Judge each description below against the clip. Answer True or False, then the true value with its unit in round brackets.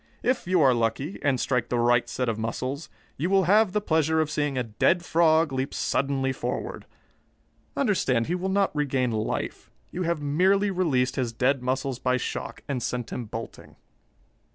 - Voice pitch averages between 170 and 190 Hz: False (140 Hz)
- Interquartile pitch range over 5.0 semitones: True (5.5 semitones)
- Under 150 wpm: False (175 wpm)